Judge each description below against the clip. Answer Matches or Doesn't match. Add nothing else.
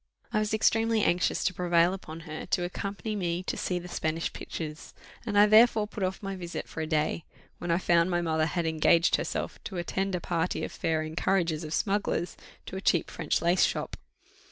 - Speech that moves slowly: Doesn't match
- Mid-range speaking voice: Matches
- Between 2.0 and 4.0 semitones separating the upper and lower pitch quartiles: Matches